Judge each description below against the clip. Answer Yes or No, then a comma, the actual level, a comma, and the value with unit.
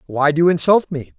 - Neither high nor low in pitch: Yes, medium, 155 Hz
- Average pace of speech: No, fast, 255 wpm